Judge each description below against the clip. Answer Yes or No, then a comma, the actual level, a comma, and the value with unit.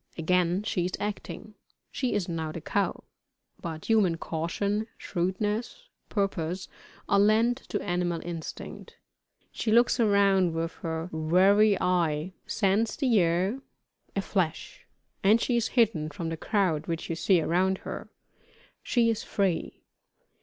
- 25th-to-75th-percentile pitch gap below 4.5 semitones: Yes, average, 4.1 semitones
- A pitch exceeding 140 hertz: Yes, high, 190 Hz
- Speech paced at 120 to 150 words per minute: Yes, slow, 135 wpm